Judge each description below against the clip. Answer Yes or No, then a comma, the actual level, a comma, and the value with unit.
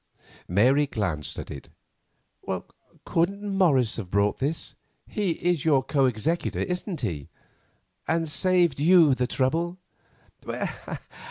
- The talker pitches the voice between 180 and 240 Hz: No, medium, 150 Hz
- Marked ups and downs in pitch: Yes, wide, 6.1 semitones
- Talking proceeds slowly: Yes, slow, 100 wpm